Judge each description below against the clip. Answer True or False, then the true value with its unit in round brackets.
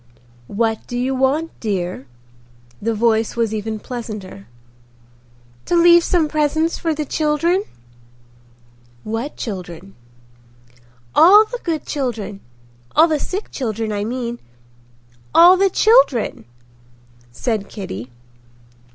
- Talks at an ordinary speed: False (100 wpm)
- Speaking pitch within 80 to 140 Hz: False (230 Hz)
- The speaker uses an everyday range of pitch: False (8.1 semitones)